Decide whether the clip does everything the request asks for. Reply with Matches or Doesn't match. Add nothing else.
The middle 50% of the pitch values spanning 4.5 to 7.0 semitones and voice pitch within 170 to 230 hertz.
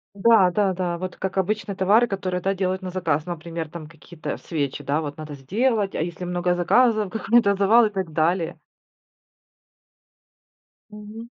Doesn't match